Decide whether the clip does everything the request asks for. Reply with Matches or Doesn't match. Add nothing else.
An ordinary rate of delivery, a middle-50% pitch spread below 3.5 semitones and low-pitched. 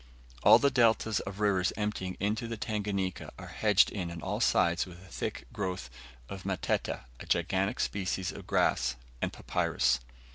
Matches